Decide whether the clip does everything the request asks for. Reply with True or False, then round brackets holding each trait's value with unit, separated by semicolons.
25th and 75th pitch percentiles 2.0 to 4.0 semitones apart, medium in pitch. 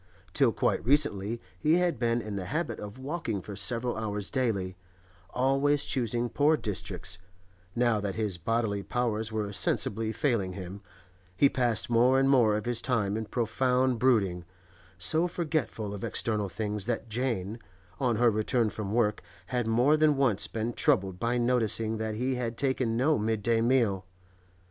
False (3.5 semitones; 115 Hz)